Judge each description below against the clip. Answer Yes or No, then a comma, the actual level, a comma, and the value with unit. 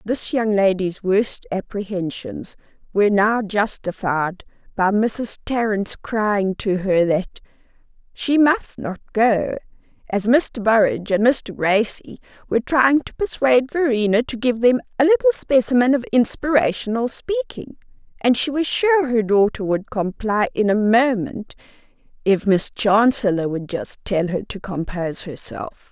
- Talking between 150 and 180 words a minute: No, average, 140 wpm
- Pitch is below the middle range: No, high, 220 Hz